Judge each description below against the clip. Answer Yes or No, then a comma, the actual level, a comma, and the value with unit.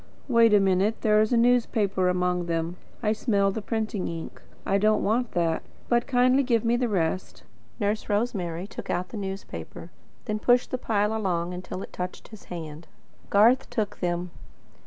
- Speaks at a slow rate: No, average, 175 wpm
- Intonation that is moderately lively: Yes, average, 4.1 semitones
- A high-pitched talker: Yes, high, 205 Hz